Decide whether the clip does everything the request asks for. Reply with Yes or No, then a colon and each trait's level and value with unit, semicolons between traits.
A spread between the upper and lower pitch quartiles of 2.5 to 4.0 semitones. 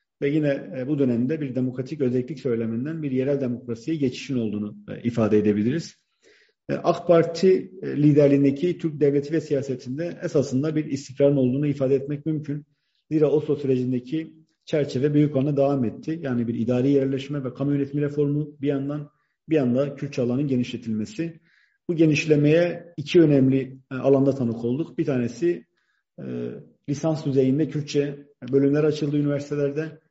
Yes: average, 2.8 semitones